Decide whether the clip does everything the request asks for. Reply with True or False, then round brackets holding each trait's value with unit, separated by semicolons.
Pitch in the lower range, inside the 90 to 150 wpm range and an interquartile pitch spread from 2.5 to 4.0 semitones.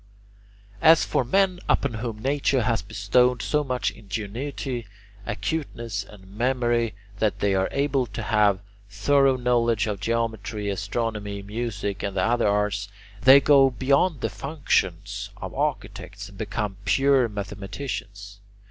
False (115 Hz; 135 wpm; 4.5 semitones)